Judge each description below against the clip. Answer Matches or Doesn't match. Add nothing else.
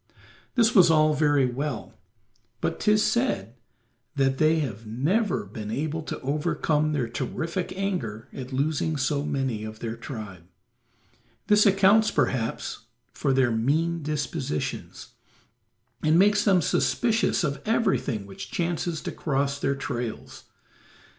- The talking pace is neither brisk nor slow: Doesn't match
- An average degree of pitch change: Doesn't match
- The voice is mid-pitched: Matches